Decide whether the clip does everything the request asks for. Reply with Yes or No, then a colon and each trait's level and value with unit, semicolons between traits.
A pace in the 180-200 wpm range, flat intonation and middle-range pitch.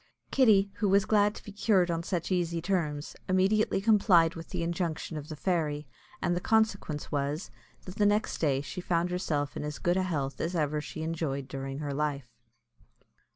No: average, 185 wpm; average, 4.4 semitones; medium, 170 Hz